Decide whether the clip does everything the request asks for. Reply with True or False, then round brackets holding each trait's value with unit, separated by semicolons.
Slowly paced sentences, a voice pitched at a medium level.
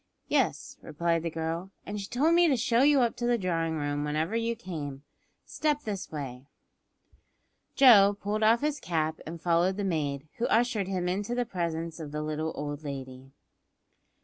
False (175 wpm; 175 Hz)